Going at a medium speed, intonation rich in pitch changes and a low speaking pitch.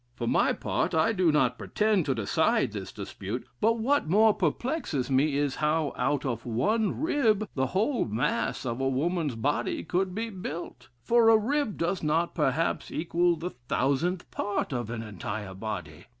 No: average, 170 wpm; wide, 8.1 semitones; medium, 160 Hz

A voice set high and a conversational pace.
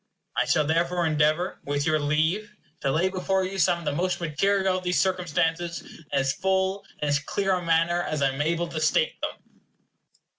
No: medium, 170 Hz; average, 195 wpm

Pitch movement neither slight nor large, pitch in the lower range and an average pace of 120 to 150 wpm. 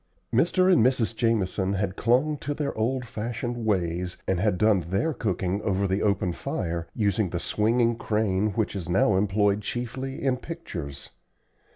No: average, 4.2 semitones; low, 105 Hz; average, 160 wpm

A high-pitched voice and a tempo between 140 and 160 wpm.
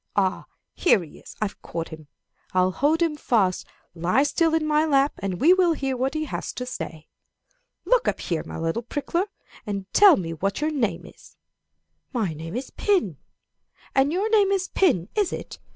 No: very high, 260 Hz; average, 185 wpm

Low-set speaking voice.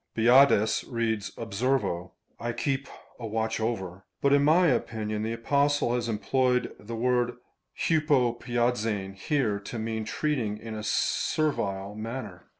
Yes: low, 115 Hz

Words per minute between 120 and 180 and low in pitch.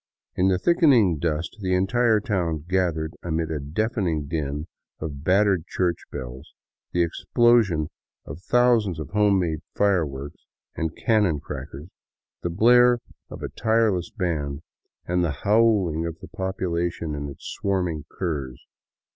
Yes: average, 140 wpm; very low, 85 Hz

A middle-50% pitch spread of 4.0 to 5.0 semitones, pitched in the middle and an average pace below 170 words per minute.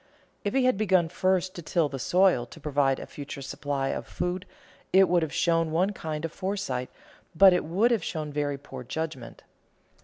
No: average, 4.5 semitones; medium, 165 Hz; average, 190 wpm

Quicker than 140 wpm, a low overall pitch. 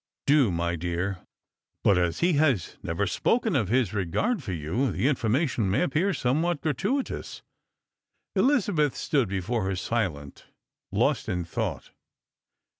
No: slow, 135 wpm; low, 115 Hz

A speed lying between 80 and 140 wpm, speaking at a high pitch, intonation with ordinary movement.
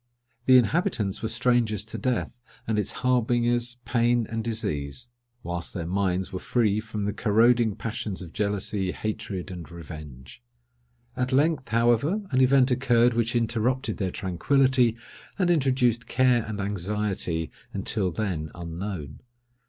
No: slow, 135 wpm; low, 110 Hz; average, 4.5 semitones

